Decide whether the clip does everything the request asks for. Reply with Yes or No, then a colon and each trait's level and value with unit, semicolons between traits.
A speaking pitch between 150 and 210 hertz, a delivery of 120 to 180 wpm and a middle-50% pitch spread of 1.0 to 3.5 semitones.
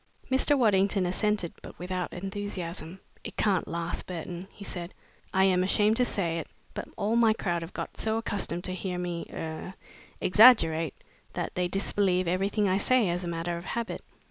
Yes: medium, 185 Hz; average, 175 wpm; average, 2.9 semitones